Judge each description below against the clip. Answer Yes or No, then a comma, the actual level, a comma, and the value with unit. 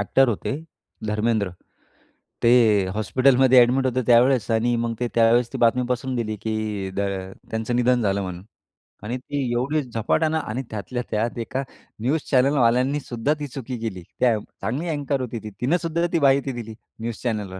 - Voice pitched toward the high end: No, low, 120 Hz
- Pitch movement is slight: No, average, 3.0 semitones